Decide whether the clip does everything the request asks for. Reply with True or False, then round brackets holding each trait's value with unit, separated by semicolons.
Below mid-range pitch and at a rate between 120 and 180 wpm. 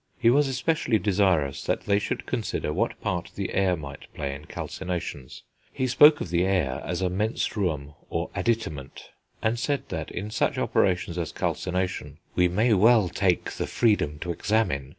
True (95 Hz; 165 wpm)